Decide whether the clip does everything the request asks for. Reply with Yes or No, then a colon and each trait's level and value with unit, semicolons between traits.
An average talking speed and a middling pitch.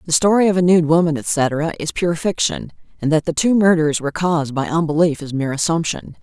No: fast, 210 wpm; medium, 165 Hz